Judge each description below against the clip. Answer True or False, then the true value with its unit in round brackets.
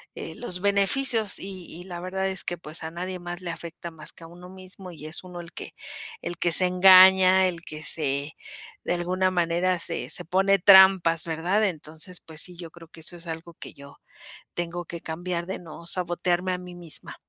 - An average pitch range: False (1.9 semitones)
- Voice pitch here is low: False (175 Hz)